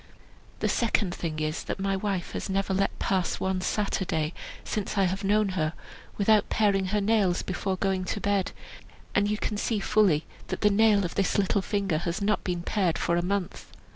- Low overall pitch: No, high, 195 Hz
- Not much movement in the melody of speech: Yes, narrow, 2.2 semitones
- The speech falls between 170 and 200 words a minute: Yes, average, 195 wpm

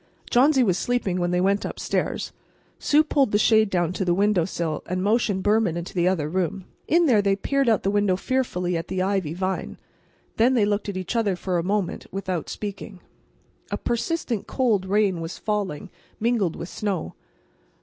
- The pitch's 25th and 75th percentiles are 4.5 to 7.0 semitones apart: No, average, 3.3 semitones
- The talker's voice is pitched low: No, high, 195 Hz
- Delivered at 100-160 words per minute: No, average, 185 wpm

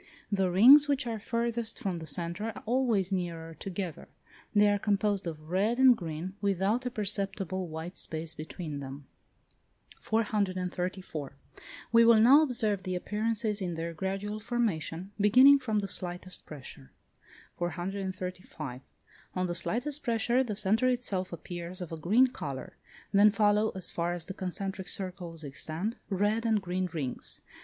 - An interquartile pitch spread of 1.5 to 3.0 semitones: No, average, 4.0 semitones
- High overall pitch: Yes, high, 195 Hz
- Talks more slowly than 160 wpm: Yes, average, 150 wpm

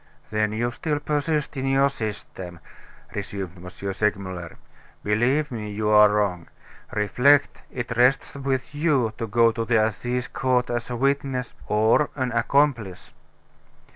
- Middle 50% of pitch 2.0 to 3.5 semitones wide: No, average, 4.3 semitones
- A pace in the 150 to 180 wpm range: No, average, 140 wpm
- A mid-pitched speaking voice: No, low, 120 Hz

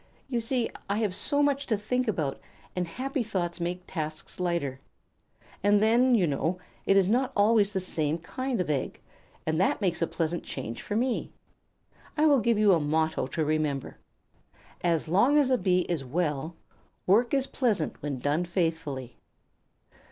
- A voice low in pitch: No, medium, 180 Hz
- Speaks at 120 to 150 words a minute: No, average, 170 wpm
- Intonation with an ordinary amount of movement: No, wide, 6.5 semitones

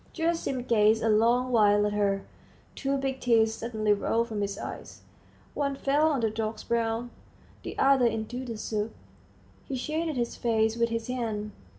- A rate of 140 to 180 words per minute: Yes, average, 170 wpm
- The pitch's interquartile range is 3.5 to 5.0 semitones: No, average, 2.9 semitones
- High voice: Yes, high, 230 Hz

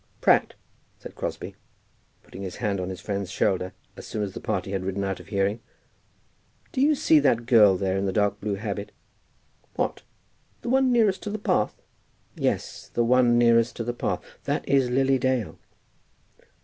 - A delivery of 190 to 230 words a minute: No, average, 175 wpm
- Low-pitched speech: Yes, low, 110 Hz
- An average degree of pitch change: Yes, average, 4.8 semitones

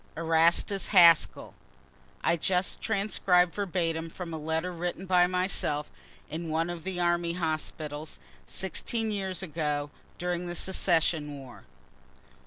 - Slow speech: Yes, slow, 120 wpm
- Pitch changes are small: Yes, narrow, 2.2 semitones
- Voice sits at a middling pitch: Yes, medium, 170 Hz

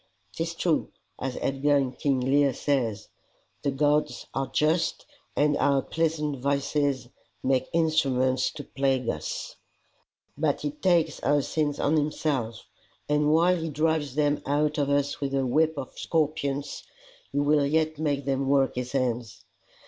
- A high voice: No, medium, 145 Hz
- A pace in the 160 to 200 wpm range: No, average, 150 wpm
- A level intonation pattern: Yes, narrow, 2.2 semitones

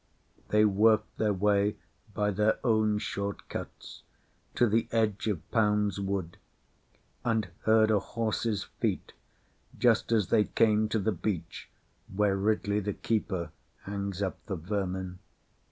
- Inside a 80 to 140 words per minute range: Yes, slow, 135 wpm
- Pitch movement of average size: No, narrow, 1.8 semitones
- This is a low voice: Yes, low, 105 Hz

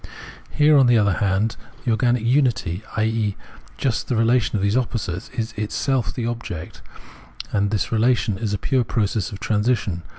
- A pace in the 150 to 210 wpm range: Yes, average, 165 wpm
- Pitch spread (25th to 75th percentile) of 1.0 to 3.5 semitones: Yes, average, 3.0 semitones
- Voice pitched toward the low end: Yes, low, 110 Hz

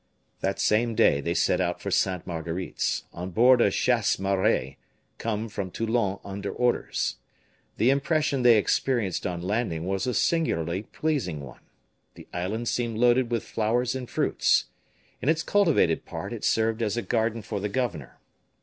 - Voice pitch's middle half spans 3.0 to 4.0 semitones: No, average, 4.7 semitones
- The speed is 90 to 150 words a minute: No, average, 160 wpm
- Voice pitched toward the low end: Yes, low, 110 Hz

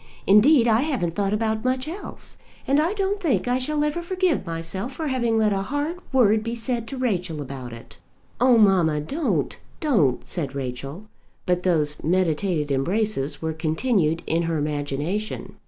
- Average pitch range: No, wide, 8.2 semitones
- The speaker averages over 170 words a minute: No, average, 165 wpm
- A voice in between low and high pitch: No, high, 205 Hz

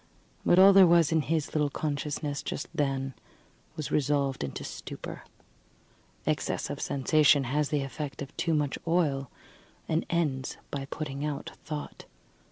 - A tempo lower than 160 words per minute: Yes, average, 150 wpm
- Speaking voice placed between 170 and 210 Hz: No, medium, 150 Hz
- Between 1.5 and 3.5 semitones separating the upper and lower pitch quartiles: Yes, narrow, 2.4 semitones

